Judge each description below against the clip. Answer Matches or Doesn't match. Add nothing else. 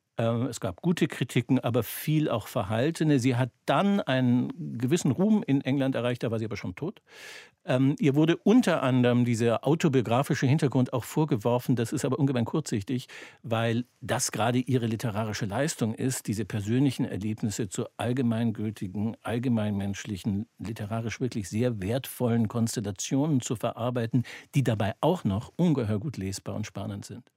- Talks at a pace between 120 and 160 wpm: Matches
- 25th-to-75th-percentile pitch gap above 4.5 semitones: Doesn't match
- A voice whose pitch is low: Matches